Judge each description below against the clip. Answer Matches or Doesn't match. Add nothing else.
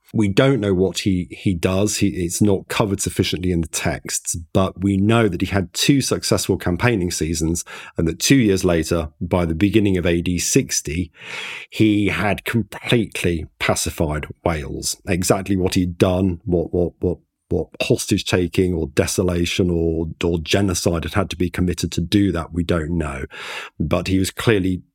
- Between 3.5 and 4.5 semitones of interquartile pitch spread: Doesn't match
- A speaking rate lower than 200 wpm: Matches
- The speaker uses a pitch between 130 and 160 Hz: Doesn't match